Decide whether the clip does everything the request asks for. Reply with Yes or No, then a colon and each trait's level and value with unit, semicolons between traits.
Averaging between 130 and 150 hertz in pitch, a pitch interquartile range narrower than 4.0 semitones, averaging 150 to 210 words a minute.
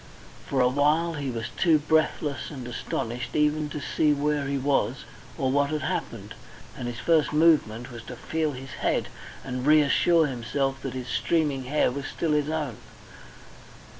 Yes: medium, 140 Hz; average, 3.1 semitones; average, 165 wpm